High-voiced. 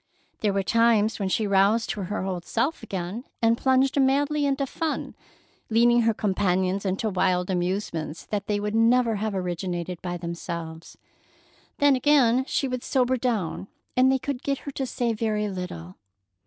Yes: high, 215 Hz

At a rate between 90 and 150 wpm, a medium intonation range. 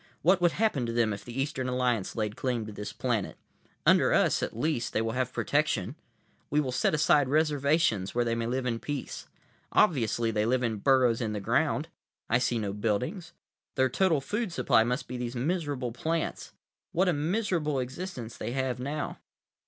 No: average, 185 wpm; average, 4.5 semitones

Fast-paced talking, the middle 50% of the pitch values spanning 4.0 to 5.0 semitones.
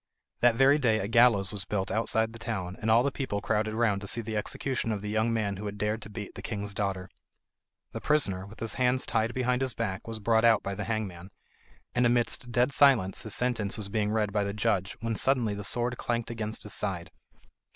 No: fast, 225 wpm; narrow, 2.6 semitones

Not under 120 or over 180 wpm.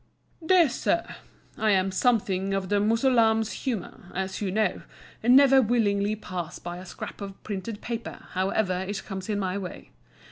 Yes: average, 155 wpm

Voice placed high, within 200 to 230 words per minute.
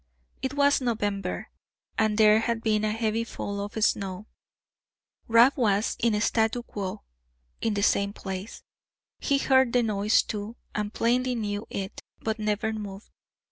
No: high, 215 Hz; average, 145 wpm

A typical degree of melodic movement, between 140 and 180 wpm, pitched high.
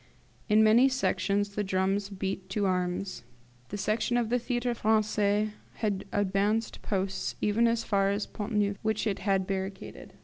No: narrow, 2.0 semitones; average, 165 wpm; high, 205 Hz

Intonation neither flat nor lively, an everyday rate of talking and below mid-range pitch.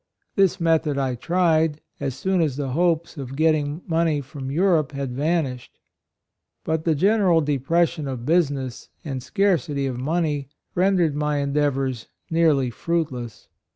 No: average, 3.6 semitones; average, 150 wpm; medium, 150 Hz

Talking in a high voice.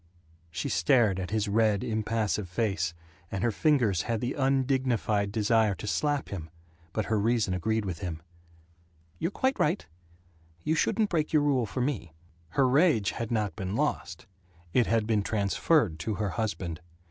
No: low, 110 Hz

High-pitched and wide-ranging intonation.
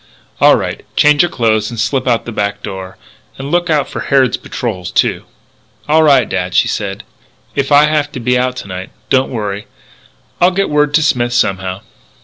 No: low, 125 Hz; wide, 6.3 semitones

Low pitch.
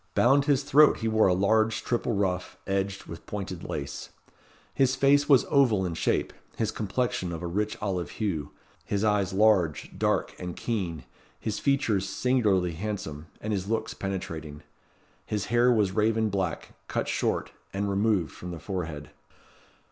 Yes: low, 100 Hz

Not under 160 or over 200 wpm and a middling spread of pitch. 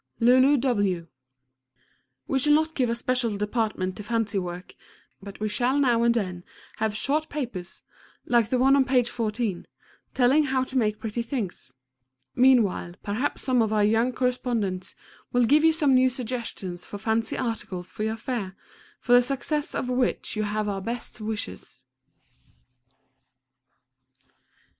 No: average, 150 wpm; average, 3.5 semitones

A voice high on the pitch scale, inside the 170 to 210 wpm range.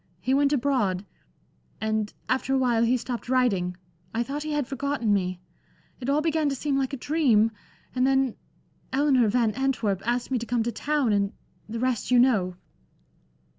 Yes: very high, 250 Hz; average, 175 wpm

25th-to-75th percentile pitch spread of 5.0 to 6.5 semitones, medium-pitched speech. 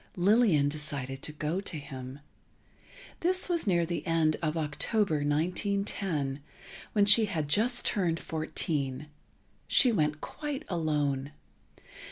Yes: wide, 5.4 semitones; medium, 160 Hz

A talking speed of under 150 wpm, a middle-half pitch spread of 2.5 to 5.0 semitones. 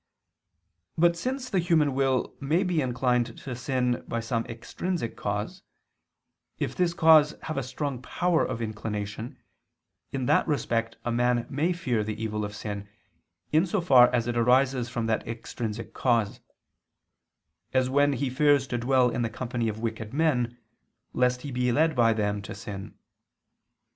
No: average, 160 wpm; average, 4.0 semitones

